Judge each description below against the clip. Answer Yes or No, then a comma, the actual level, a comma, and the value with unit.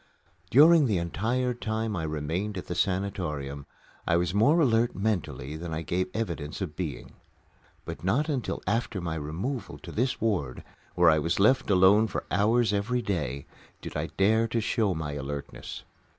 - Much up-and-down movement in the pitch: Yes, wide, 6.0 semitones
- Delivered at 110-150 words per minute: No, average, 165 wpm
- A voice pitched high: No, very low, 95 Hz